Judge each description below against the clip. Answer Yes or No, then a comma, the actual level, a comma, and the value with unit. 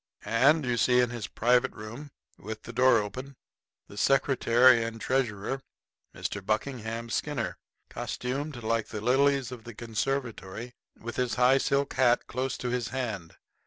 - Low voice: Yes, low, 120 Hz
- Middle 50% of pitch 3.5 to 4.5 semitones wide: No, narrow, 2.5 semitones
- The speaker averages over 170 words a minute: No, average, 150 wpm